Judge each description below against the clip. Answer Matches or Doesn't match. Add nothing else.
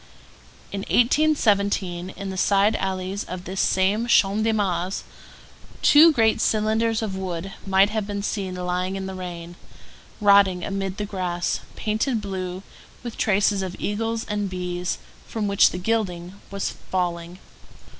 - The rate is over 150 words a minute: Doesn't match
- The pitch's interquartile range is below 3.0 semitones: Matches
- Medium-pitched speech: Doesn't match